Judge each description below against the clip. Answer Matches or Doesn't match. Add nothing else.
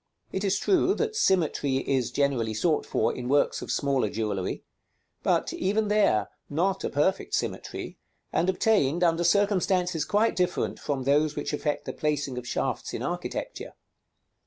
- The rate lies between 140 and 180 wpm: Matches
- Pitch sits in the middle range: Matches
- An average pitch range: Doesn't match